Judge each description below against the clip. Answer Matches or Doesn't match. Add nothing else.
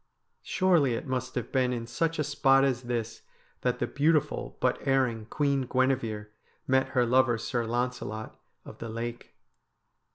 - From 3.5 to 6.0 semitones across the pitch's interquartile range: Doesn't match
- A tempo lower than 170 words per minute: Matches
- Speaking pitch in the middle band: Doesn't match